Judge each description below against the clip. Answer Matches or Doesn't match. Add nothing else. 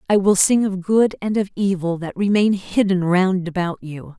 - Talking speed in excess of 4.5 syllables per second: Matches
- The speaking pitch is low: Doesn't match